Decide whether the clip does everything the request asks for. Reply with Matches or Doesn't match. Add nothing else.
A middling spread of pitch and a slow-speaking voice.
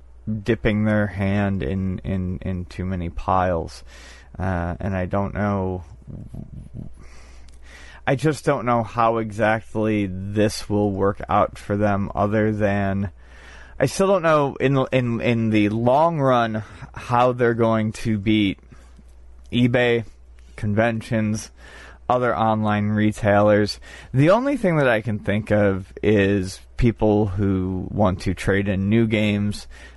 Matches